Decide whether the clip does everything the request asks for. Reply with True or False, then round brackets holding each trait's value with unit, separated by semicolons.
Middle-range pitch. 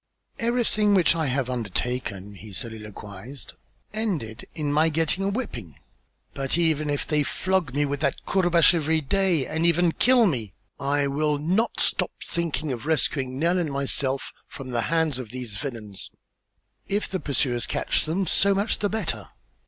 True (150 Hz)